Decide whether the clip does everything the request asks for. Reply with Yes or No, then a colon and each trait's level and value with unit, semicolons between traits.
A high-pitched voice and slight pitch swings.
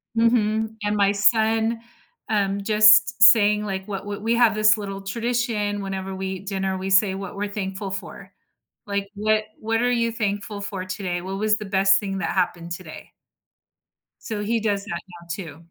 Yes: high, 205 Hz; narrow, 2.0 semitones